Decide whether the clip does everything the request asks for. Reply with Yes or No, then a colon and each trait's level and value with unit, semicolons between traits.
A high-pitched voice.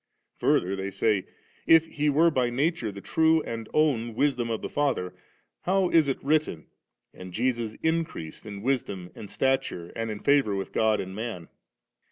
No: low, 120 Hz